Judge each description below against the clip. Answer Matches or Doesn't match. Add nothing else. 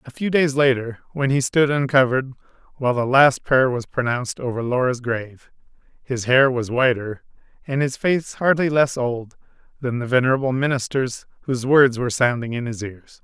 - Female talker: Doesn't match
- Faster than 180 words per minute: Doesn't match